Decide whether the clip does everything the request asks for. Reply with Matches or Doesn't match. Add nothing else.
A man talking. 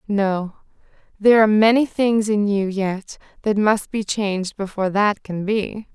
Doesn't match